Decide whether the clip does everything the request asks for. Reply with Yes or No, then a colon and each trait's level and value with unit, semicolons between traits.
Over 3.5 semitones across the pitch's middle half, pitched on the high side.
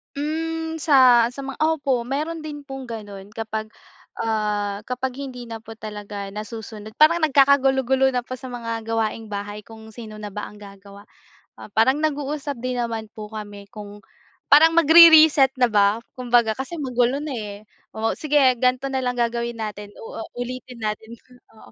Yes: average, 4.1 semitones; high, 240 Hz